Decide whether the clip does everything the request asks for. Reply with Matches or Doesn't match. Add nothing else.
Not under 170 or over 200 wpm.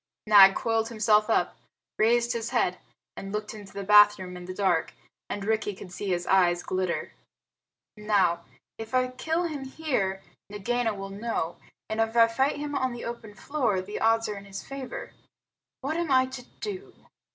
Matches